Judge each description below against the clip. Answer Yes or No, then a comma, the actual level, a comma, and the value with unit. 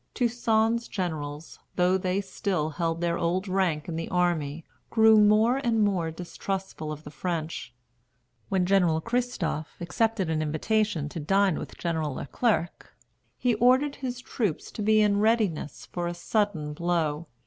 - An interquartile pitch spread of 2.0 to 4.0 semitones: No, average, 5.1 semitones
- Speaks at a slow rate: No, average, 150 wpm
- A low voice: No, medium, 180 Hz